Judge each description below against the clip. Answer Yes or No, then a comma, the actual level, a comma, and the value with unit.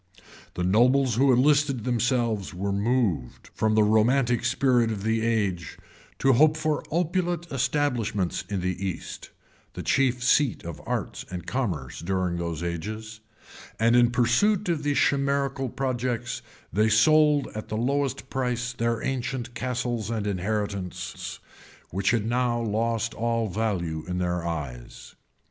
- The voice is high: No, low, 115 Hz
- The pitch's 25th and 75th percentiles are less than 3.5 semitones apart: No, average, 4.7 semitones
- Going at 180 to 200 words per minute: No, average, 140 wpm